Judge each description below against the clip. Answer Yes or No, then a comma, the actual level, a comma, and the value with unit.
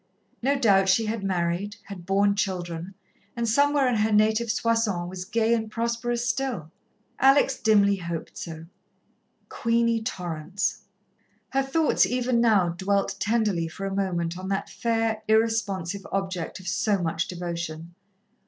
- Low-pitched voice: No, high, 200 Hz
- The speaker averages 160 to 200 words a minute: No, average, 140 wpm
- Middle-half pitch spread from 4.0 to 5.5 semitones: Yes, average, 4.3 semitones